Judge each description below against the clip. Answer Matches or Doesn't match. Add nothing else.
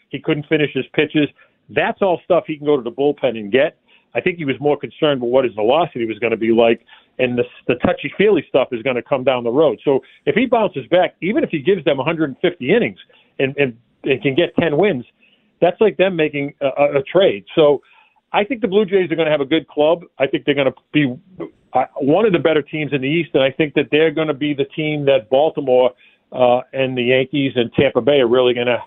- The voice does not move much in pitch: Doesn't match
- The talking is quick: Matches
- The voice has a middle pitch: Matches